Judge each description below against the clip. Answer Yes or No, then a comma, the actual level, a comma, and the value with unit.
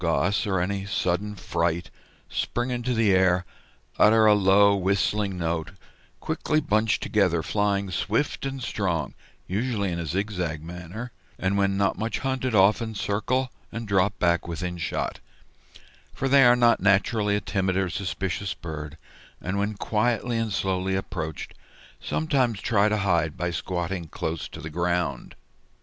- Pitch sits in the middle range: No, low, 100 Hz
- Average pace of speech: Yes, average, 150 wpm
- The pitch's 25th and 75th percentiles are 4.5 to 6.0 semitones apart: No, average, 3.7 semitones